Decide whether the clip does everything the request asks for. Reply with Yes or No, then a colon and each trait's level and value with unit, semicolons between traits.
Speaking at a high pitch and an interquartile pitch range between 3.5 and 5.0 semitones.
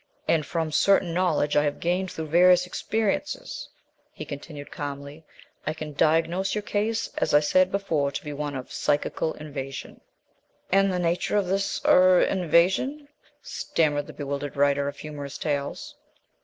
No: medium, 160 Hz; average, 4.2 semitones